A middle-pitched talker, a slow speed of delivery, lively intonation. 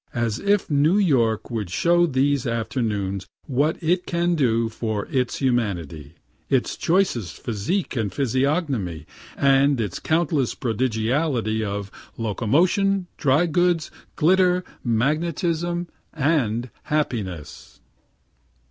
No: low, 130 Hz; slow, 105 wpm; wide, 6.9 semitones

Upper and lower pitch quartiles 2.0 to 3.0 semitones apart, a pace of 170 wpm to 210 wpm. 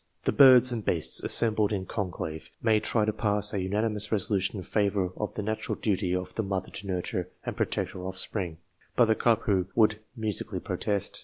Yes: average, 2.7 semitones; average, 185 wpm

